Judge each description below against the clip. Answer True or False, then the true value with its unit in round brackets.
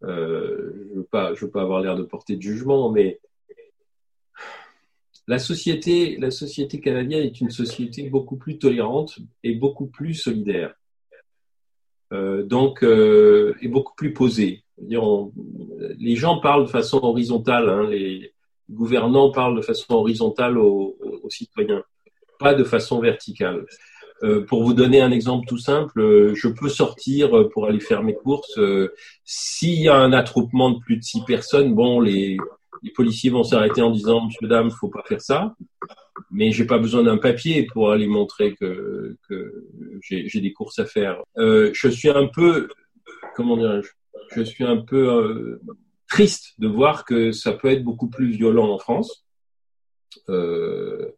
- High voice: False (135 Hz)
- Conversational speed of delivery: True (160 wpm)